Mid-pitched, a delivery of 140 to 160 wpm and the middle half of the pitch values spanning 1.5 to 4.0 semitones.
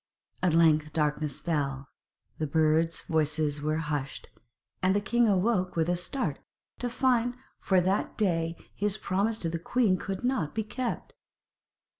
No: medium, 175 Hz; average, 155 wpm; wide, 5.4 semitones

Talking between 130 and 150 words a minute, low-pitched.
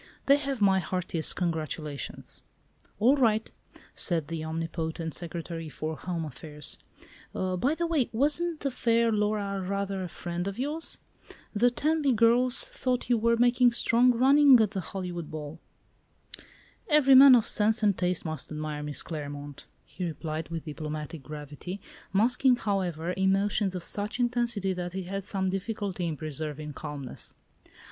No: average, 145 wpm; high, 190 Hz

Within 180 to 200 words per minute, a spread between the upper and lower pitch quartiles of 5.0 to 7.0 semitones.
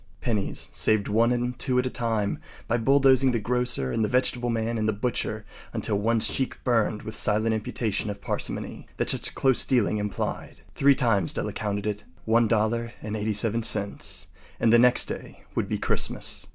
No: average, 190 wpm; narrow, 2.4 semitones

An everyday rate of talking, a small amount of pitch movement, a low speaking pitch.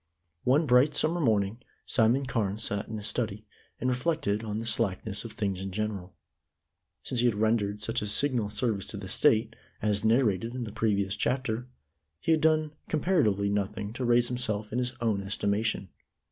No: average, 180 wpm; average, 3.5 semitones; low, 110 Hz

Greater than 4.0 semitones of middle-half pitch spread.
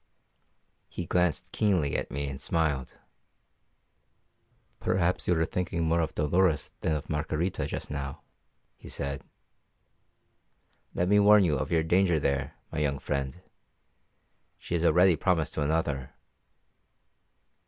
No: average, 3.7 semitones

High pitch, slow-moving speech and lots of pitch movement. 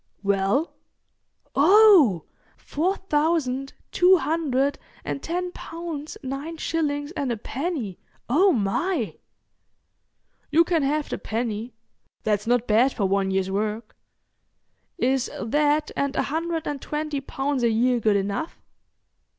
Yes: very high, 275 Hz; slow, 125 wpm; wide, 6.2 semitones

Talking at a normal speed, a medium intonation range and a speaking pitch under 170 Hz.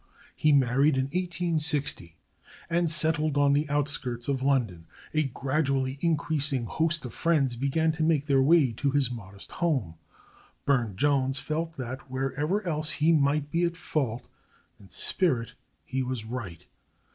Yes: average, 145 wpm; average, 3.4 semitones; medium, 140 Hz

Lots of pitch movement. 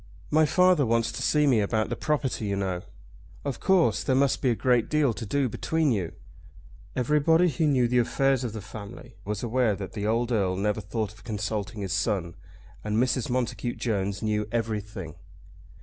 No: average, 4.3 semitones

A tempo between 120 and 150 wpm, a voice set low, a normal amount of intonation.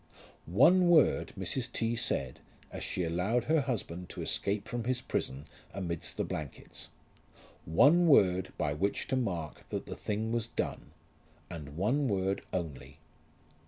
No: average, 145 wpm; low, 100 Hz; wide, 6.5 semitones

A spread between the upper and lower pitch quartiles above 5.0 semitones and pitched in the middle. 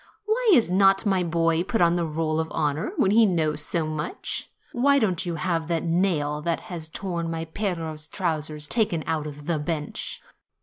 No: average, 3.3 semitones; medium, 165 Hz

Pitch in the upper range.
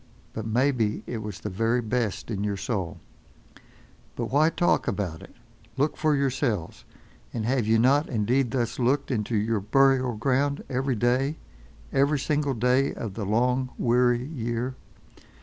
No: low, 125 Hz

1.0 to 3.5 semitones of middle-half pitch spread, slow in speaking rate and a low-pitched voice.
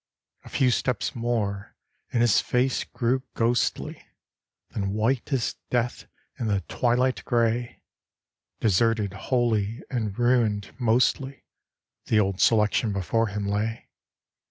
Yes: average, 2.8 semitones; slow, 115 wpm; low, 115 Hz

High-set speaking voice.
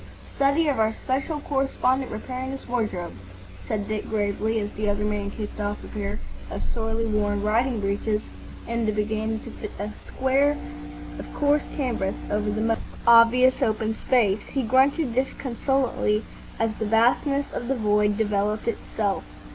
Yes: high, 225 Hz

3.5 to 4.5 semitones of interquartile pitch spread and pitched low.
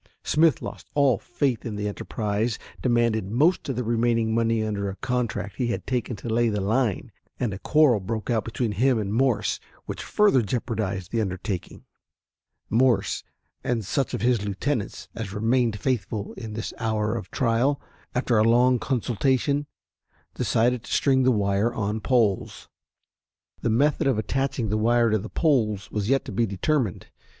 No: average, 3.1 semitones; low, 115 Hz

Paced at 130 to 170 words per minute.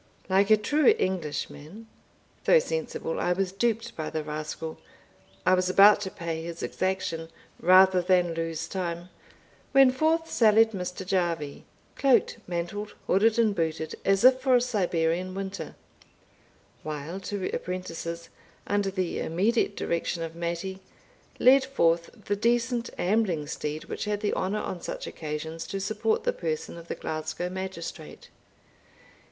Yes: average, 140 wpm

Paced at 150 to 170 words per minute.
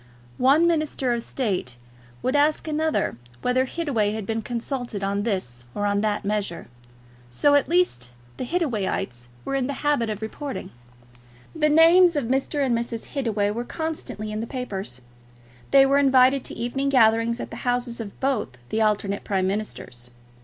Yes: average, 165 wpm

